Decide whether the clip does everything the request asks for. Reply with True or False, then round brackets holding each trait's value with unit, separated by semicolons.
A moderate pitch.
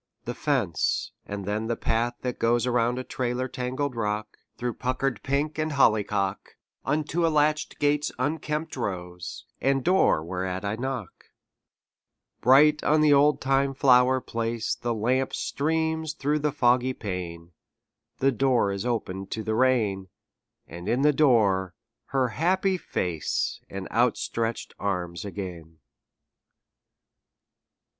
False (125 Hz)